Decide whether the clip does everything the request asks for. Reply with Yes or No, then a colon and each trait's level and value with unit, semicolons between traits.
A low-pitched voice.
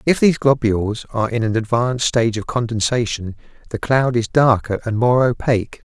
Yes: low, 120 Hz